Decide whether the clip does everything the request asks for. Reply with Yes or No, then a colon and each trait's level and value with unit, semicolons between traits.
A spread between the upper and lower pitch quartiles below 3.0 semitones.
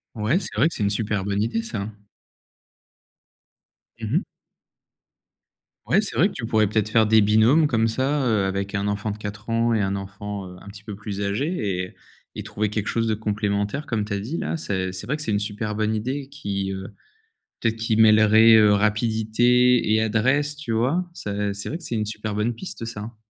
Yes: narrow, 2.4 semitones